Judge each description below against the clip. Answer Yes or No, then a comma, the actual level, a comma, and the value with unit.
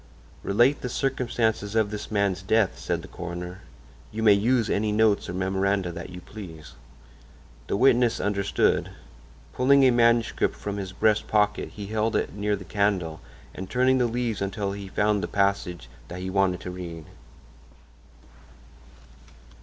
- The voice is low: Yes, low, 100 Hz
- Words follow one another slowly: No, average, 155 wpm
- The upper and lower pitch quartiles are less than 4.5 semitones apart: Yes, average, 2.9 semitones